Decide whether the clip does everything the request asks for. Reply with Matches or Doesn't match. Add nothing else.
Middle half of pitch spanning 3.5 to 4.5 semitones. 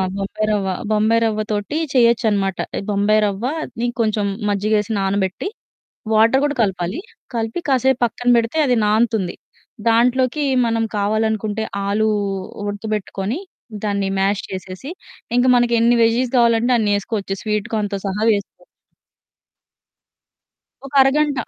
Doesn't match